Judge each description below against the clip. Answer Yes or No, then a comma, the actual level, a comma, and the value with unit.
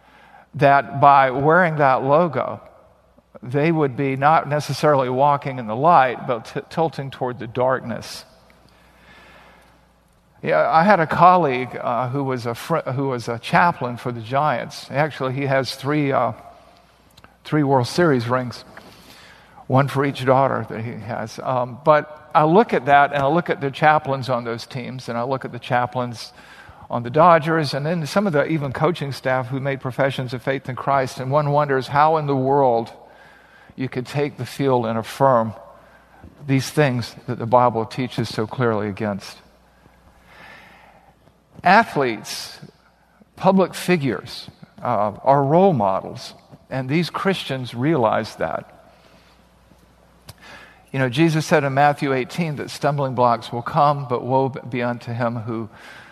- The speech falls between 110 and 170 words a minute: Yes, average, 155 wpm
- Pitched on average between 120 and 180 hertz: Yes, low, 135 Hz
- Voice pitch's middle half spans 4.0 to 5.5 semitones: No, average, 3.2 semitones